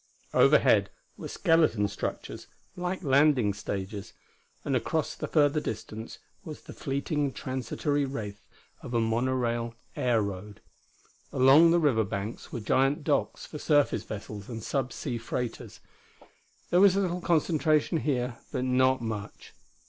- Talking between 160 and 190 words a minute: No, slow, 135 wpm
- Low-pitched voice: Yes, low, 130 Hz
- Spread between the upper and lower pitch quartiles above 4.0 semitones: Yes, average, 5.1 semitones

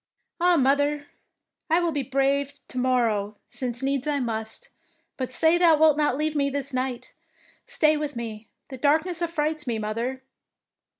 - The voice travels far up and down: No, average, 3.4 semitones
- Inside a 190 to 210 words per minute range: No, average, 175 wpm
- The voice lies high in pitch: Yes, very high, 280 Hz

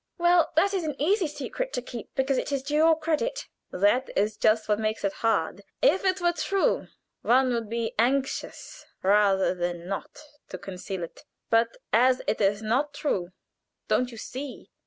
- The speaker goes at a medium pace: Yes, average, 180 wpm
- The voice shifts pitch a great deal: Yes, wide, 6.7 semitones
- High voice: Yes, very high, 250 Hz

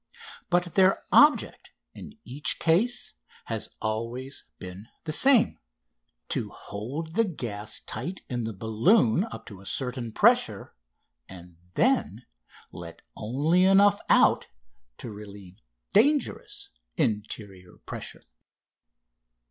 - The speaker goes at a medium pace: No, slow, 110 wpm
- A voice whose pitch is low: Yes, low, 125 Hz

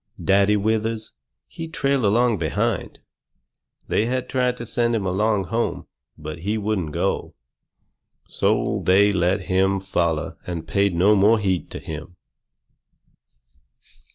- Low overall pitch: Yes, low, 100 Hz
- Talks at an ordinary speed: No, slow, 125 wpm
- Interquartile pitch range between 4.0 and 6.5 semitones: No, average, 3.6 semitones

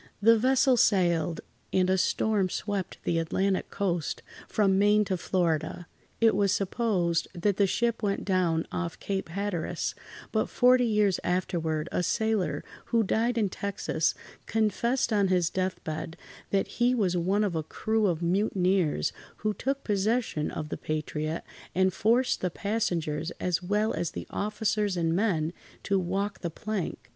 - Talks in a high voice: Yes, high, 195 Hz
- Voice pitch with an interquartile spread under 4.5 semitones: Yes, average, 3.7 semitones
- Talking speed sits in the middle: Yes, average, 150 wpm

